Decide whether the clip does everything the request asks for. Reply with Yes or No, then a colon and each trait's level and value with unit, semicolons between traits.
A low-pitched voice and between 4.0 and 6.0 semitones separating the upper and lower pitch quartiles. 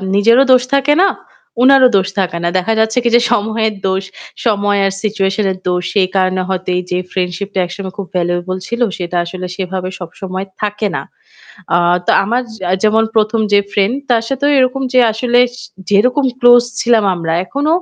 No: high, 205 Hz; average, 4.3 semitones